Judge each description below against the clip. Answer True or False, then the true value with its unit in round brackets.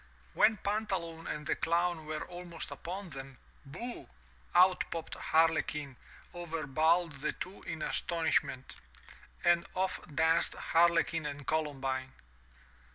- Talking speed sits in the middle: False (120 wpm)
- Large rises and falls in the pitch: False (2.7 semitones)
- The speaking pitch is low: False (165 Hz)